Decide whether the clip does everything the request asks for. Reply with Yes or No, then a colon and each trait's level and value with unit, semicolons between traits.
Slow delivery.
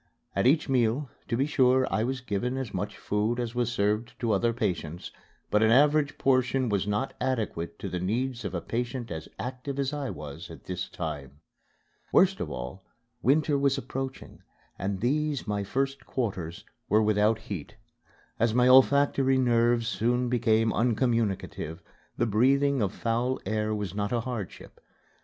No: average, 165 wpm